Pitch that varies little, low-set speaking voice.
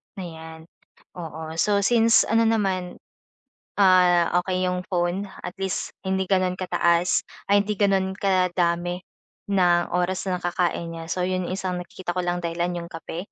No: narrow, 1.6 semitones; medium, 180 Hz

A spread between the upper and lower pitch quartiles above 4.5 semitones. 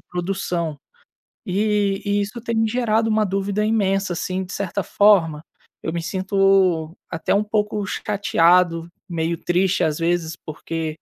No: average, 3.4 semitones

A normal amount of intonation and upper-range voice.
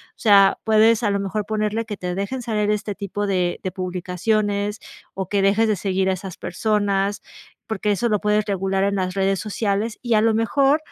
No: narrow, 1.9 semitones; high, 205 Hz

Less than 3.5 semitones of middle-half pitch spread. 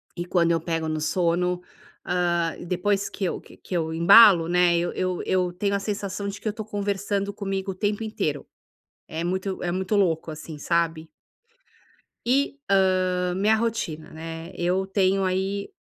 Yes: average, 2.8 semitones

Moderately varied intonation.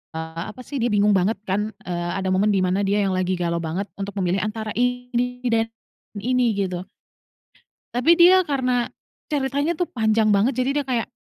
Yes: average, 4.6 semitones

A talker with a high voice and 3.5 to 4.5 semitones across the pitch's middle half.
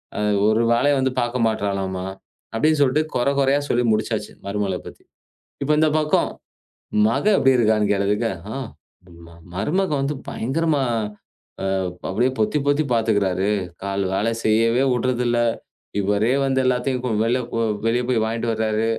No: low, 115 Hz; average, 3.9 semitones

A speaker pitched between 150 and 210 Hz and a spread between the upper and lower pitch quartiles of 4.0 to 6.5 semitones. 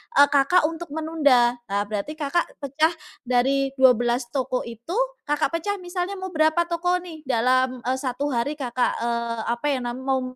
No: very high, 275 Hz; average, 4.5 semitones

